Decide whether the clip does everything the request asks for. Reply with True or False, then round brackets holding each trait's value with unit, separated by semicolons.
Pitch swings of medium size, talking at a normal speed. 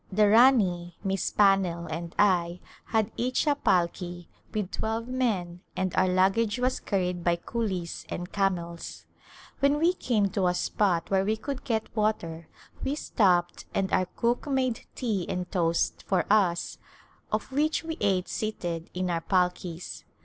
True (4.3 semitones; 155 wpm)